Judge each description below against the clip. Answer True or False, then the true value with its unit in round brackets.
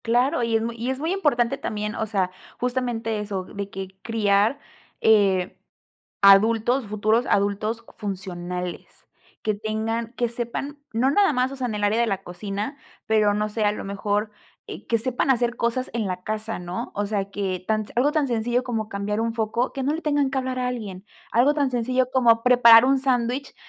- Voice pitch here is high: True (225 Hz)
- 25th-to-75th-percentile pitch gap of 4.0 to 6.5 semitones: False (3.4 semitones)